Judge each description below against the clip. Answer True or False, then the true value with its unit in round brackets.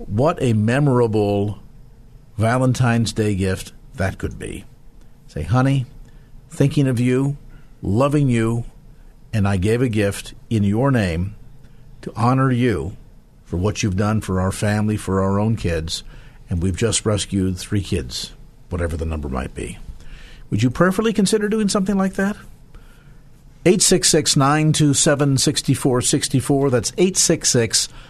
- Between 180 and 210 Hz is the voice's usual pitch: False (120 Hz)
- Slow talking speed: True (130 wpm)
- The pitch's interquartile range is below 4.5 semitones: False (5.3 semitones)